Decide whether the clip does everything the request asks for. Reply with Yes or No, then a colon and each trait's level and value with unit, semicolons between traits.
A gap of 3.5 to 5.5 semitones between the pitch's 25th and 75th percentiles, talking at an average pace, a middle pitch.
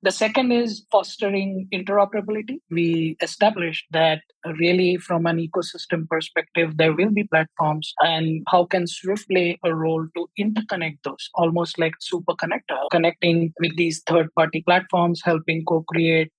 No: average, 2.7 semitones; average, 145 wpm; medium, 170 Hz